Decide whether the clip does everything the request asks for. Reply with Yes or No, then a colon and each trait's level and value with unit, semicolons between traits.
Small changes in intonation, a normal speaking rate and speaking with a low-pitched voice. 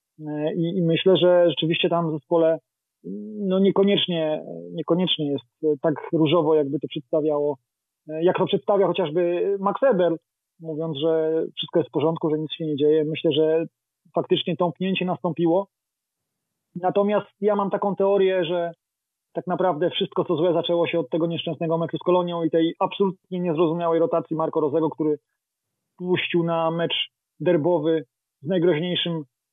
No: narrow, 2.3 semitones; average, 145 wpm; medium, 170 Hz